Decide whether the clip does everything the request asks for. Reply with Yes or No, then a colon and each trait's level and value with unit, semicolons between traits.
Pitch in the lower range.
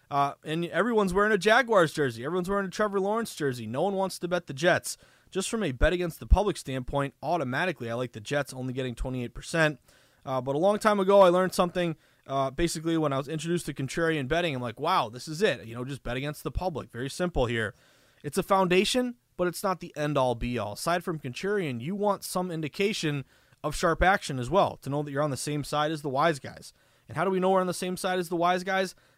No: medium, 160 Hz